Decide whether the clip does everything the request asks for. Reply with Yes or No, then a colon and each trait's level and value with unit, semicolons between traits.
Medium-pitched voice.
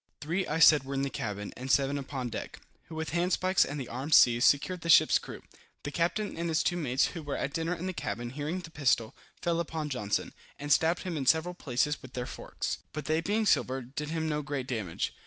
Yes: medium, 150 Hz